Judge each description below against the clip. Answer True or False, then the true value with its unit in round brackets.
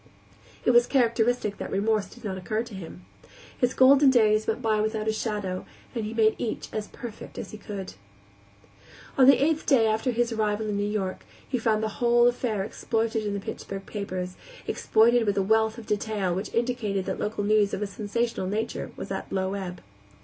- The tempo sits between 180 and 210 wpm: True (200 wpm)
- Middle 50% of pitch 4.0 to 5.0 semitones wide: False (2.6 semitones)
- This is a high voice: True (215 Hz)